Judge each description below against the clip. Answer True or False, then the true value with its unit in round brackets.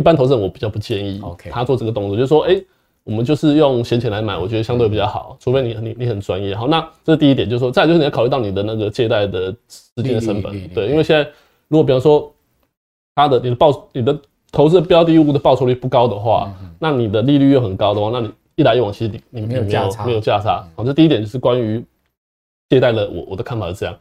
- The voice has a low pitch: True (120 Hz)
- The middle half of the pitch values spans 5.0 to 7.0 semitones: True (5.3 semitones)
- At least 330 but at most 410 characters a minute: True (380 characters per minute)